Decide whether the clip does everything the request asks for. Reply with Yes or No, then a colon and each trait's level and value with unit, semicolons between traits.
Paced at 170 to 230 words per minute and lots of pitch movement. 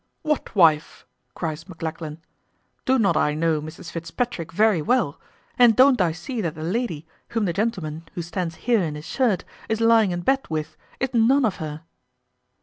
Yes: average, 175 wpm; wide, 6.3 semitones